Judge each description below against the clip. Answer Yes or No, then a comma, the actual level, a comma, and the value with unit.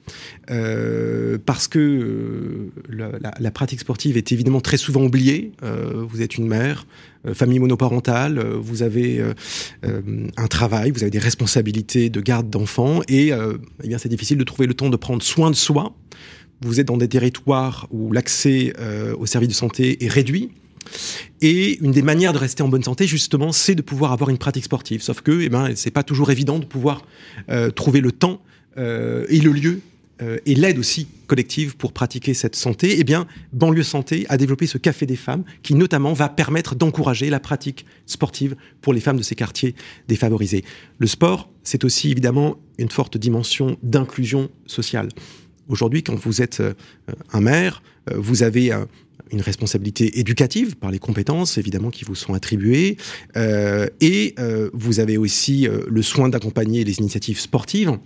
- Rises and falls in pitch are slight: No, average, 4.3 semitones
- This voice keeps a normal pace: Yes, average, 185 wpm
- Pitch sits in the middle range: No, low, 130 Hz